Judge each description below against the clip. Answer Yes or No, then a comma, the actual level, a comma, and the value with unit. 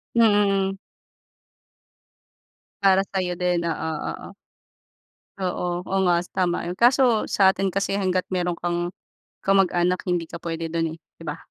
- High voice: No, medium, 180 Hz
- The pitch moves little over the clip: Yes, narrow, 2.0 semitones